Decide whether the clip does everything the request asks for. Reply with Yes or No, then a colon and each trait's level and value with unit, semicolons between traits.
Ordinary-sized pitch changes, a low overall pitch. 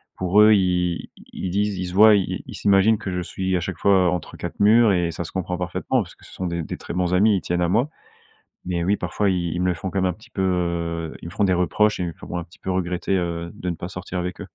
No: narrow, 1.9 semitones; very low, 90 Hz